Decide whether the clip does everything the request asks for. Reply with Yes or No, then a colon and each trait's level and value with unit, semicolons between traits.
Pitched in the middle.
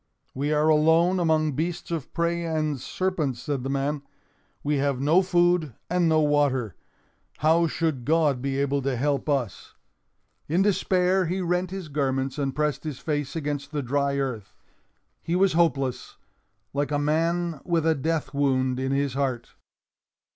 Yes: medium, 150 Hz